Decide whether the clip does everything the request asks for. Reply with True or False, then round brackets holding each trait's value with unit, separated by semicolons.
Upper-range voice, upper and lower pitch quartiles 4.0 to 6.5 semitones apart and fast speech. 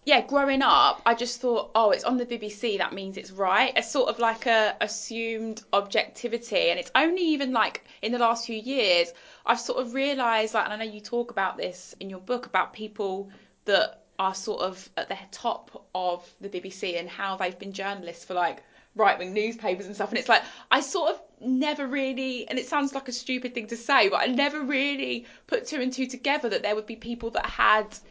True (230 Hz; 4.6 semitones; 220 wpm)